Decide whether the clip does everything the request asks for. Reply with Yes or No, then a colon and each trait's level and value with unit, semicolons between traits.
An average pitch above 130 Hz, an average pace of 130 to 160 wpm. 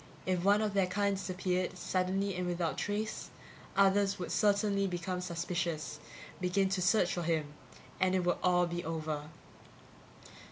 Yes: medium, 185 Hz; average, 150 wpm